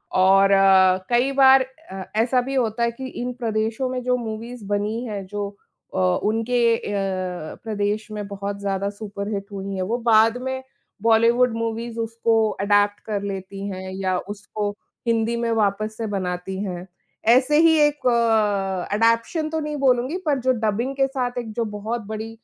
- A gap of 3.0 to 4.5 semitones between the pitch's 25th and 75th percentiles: Yes, average, 3.5 semitones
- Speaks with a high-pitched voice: Yes, high, 220 Hz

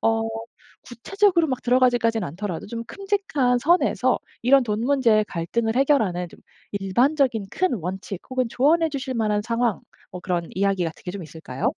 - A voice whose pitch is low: No, high, 230 Hz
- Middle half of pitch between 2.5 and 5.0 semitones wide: No, wide, 5.6 semitones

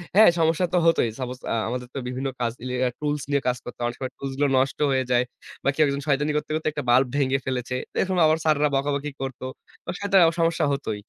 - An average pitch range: Yes, average, 3.1 semitones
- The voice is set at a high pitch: No, medium, 140 Hz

